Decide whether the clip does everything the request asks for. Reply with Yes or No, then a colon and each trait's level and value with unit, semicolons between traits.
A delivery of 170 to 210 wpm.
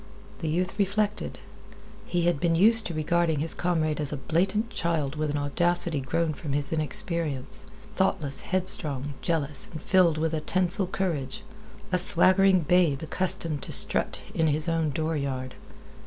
No: average, 155 wpm